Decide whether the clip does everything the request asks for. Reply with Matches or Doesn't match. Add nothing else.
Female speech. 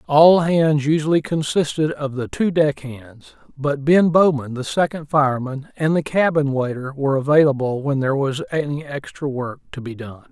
Doesn't match